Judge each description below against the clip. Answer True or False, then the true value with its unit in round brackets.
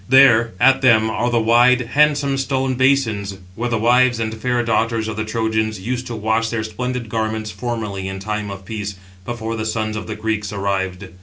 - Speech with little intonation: True (2.2 semitones)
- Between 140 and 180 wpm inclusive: False (190 wpm)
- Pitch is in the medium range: False (110 Hz)